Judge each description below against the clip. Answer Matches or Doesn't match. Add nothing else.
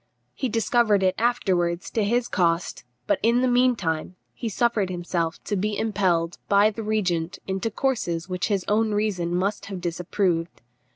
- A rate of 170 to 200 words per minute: Doesn't match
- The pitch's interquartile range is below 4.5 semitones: Matches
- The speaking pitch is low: Doesn't match